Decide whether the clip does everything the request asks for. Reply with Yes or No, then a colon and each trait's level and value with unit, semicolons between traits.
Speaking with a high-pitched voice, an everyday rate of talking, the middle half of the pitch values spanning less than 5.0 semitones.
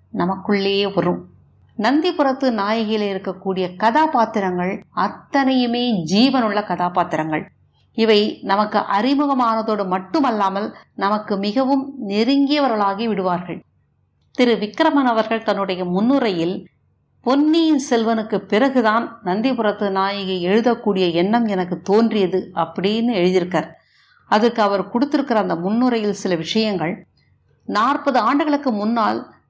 Yes: high, 210 Hz; average, 85 wpm; average, 4.2 semitones